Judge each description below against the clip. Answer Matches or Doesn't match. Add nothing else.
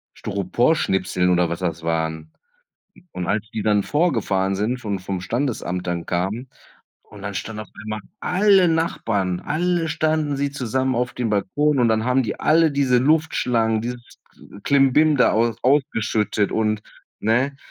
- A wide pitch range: Matches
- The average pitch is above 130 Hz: Doesn't match